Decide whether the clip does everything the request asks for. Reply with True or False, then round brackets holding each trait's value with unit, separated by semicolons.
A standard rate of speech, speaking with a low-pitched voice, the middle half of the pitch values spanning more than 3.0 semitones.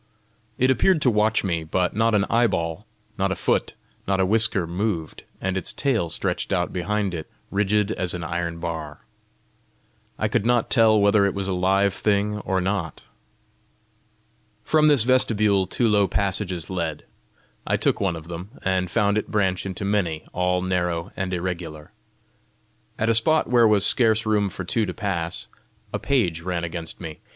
True (170 wpm; 95 Hz; 3.4 semitones)